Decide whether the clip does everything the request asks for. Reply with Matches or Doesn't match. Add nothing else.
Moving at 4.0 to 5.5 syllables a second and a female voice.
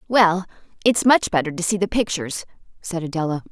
Doesn't match